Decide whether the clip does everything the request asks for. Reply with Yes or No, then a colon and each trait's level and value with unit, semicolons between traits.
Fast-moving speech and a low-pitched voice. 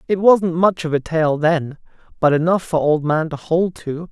No: fast, 220 wpm; medium, 165 Hz